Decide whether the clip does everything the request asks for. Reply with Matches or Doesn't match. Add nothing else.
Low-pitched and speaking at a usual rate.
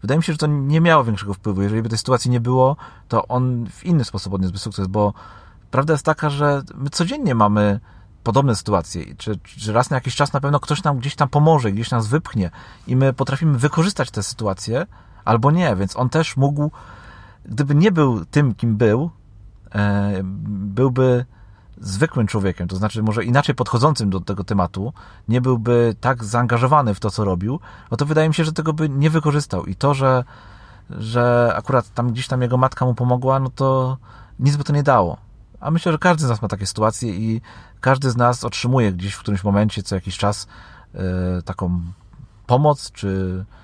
Doesn't match